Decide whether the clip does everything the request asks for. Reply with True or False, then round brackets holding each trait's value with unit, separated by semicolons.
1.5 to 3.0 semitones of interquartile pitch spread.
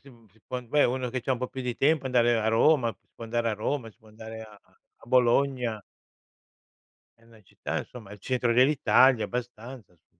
True (2.4 semitones)